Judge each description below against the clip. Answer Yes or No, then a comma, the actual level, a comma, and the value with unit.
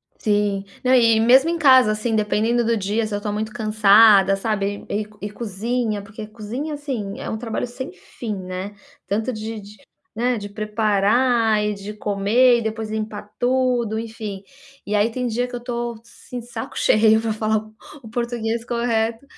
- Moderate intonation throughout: No, narrow, 2.3 semitones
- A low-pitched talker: No, high, 220 Hz